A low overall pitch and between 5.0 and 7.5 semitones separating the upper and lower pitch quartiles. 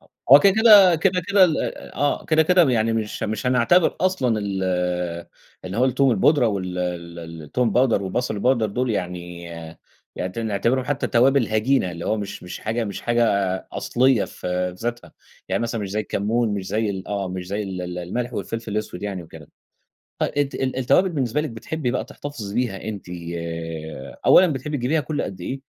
Yes: low, 115 Hz; wide, 5.4 semitones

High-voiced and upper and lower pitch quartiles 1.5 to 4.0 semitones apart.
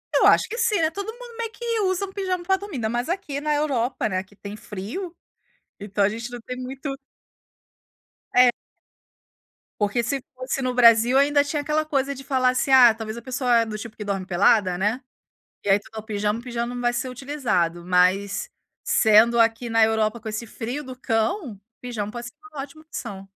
No: high, 245 Hz; average, 4.9 semitones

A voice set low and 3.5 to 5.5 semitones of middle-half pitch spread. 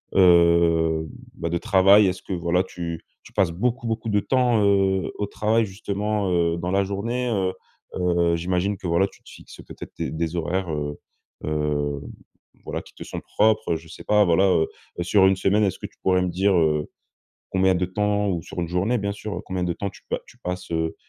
No: very low, 95 Hz; average, 3.1 semitones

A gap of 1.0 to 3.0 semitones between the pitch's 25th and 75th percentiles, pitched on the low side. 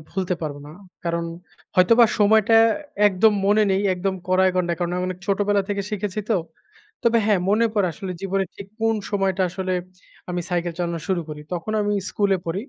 No: narrow, 2.5 semitones; high, 195 Hz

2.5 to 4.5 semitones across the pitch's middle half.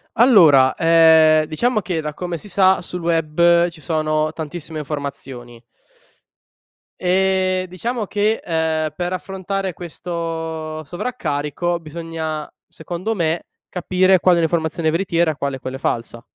Yes: average, 2.8 semitones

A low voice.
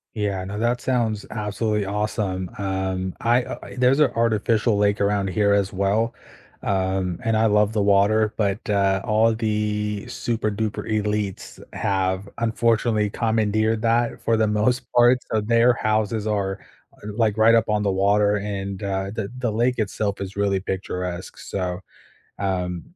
Yes: low, 105 Hz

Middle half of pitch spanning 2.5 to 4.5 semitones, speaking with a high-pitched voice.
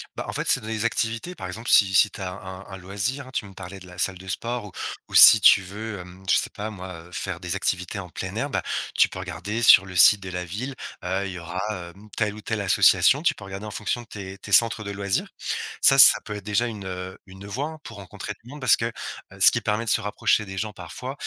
No: average, 3.0 semitones; low, 100 Hz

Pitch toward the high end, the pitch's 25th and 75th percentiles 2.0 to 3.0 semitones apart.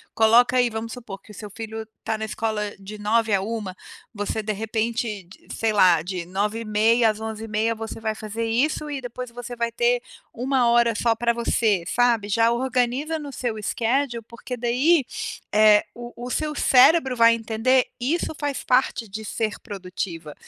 Yes: high, 225 Hz; narrow, 2.4 semitones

